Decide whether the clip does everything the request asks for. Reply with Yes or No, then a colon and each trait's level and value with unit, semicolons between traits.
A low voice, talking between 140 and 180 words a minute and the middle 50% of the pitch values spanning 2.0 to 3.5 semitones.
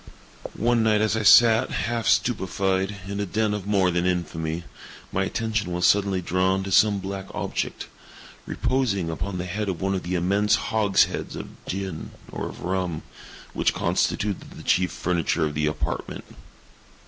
Yes: very low, 95 Hz; average, 160 wpm; average, 2.8 semitones